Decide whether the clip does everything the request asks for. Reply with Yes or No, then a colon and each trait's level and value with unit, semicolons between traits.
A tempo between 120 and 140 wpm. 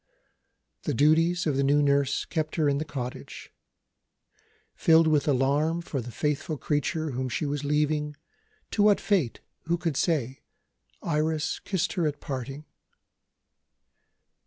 Yes: slow, 135 wpm